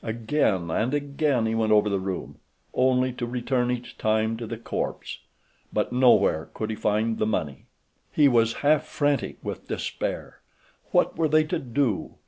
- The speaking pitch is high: No, low, 120 Hz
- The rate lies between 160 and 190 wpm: Yes, average, 170 wpm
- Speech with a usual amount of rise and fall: Yes, average, 4.0 semitones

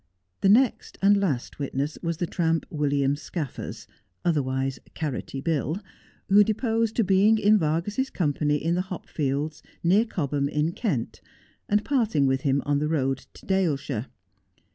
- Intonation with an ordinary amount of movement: No, wide, 5.8 semitones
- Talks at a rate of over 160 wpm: No, average, 150 wpm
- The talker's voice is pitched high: No, medium, 160 Hz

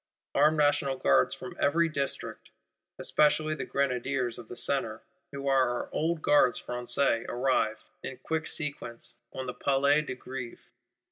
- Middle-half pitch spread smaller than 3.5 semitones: Yes, average, 3.1 semitones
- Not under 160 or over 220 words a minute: No, average, 145 wpm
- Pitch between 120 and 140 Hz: Yes, low, 135 Hz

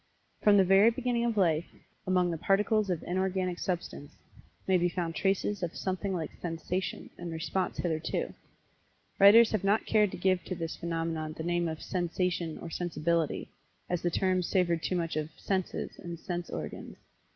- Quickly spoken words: No, average, 170 wpm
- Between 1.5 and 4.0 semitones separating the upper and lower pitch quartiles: Yes, narrow, 2.5 semitones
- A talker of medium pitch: Yes, medium, 180 Hz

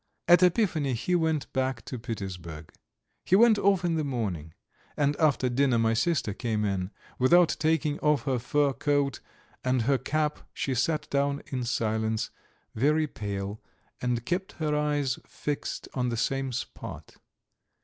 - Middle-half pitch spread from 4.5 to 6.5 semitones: Yes, average, 4.8 semitones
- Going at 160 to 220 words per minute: No, average, 150 wpm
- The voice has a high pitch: No, low, 135 Hz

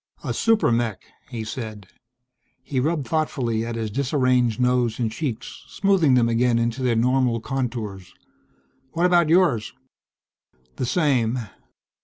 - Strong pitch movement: No, average, 3.3 semitones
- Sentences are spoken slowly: Yes, slow, 130 wpm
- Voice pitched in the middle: No, low, 125 Hz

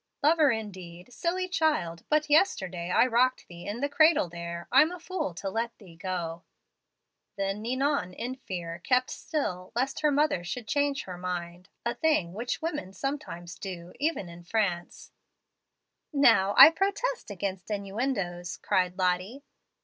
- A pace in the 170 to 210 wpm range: No, average, 150 wpm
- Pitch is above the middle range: Yes, high, 210 Hz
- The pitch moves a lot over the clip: Yes, wide, 8.1 semitones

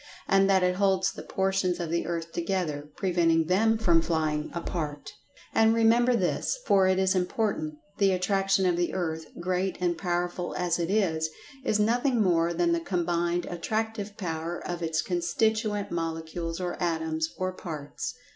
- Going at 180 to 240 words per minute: No, average, 155 wpm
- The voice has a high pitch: No, medium, 180 Hz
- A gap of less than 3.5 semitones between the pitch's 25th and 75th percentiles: Yes, average, 2.8 semitones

